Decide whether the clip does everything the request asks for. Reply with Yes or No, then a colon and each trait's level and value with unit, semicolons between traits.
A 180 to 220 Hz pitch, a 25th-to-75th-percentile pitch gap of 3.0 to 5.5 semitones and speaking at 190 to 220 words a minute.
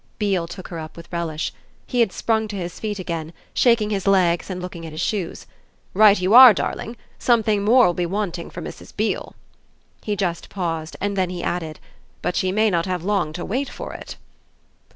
Yes: medium, 185 Hz; average, 3.6 semitones; average, 195 wpm